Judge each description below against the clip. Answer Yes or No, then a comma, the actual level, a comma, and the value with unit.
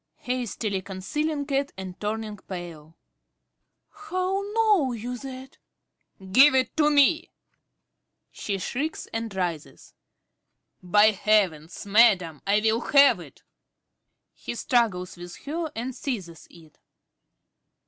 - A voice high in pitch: Yes, high, 225 Hz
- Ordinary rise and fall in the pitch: No, wide, 6.8 semitones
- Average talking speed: No, slow, 115 wpm